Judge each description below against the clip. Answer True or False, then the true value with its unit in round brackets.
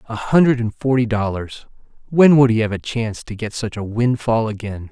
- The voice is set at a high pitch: False (115 Hz)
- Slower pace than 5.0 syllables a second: False (5.3 syllables/s)